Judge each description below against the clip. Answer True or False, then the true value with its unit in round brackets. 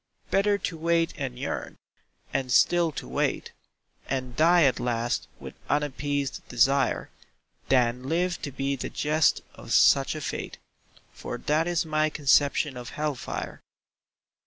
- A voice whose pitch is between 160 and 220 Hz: False (145 Hz)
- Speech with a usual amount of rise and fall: True (3.7 semitones)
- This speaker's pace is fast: False (140 wpm)